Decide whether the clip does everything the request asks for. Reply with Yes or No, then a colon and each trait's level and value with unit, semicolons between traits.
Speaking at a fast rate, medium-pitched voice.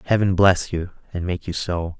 No: fast, 210 wpm; very low, 90 Hz